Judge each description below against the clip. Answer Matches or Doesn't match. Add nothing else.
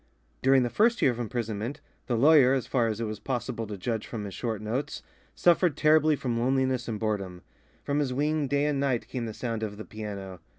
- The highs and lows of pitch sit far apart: Doesn't match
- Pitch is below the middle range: Matches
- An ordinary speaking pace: Doesn't match